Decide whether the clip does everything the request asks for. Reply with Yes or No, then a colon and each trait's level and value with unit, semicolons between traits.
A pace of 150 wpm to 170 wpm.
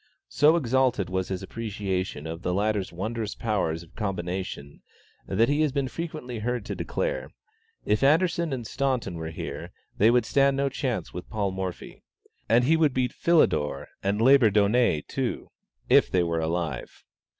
Yes: average, 160 wpm